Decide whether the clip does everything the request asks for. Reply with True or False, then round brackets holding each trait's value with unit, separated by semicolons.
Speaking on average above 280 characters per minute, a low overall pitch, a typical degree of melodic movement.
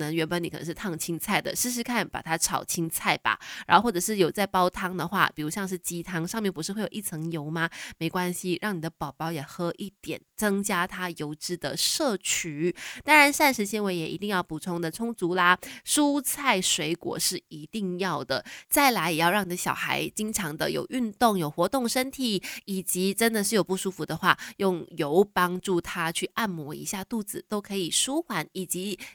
False (290 characters per minute; 180 Hz; 3.9 semitones)